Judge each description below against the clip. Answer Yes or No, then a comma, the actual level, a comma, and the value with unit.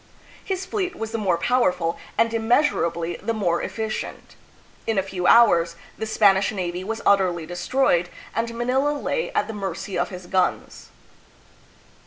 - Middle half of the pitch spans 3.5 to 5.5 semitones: Yes, average, 4.6 semitones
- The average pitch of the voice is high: Yes, high, 210 Hz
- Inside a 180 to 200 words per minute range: No, average, 155 wpm